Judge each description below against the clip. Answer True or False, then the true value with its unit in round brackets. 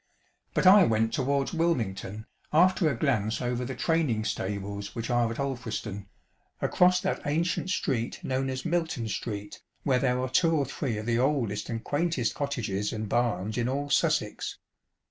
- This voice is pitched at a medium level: False (125 Hz)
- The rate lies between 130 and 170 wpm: True (165 wpm)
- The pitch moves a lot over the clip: False (5.0 semitones)